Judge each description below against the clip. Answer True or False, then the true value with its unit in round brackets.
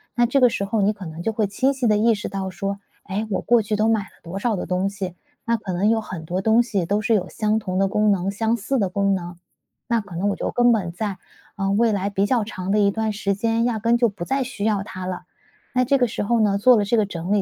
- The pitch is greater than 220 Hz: False (205 Hz)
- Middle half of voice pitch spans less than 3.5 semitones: True (2.7 semitones)